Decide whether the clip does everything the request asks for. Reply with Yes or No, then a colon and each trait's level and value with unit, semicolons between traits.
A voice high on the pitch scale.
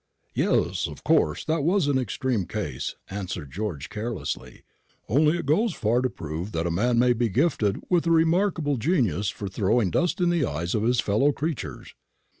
No: low, 120 Hz